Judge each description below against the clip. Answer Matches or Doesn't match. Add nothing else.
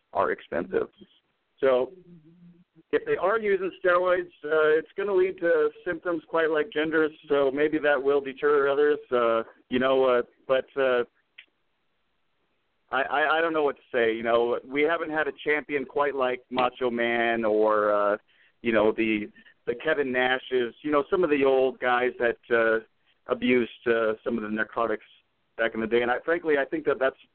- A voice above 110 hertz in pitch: Matches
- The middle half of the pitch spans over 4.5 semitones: Matches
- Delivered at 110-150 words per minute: Doesn't match